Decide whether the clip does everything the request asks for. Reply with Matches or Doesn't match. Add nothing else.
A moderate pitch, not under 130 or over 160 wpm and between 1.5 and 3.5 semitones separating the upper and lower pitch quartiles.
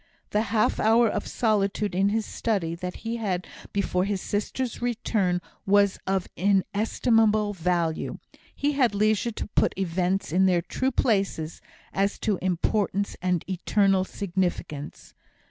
Doesn't match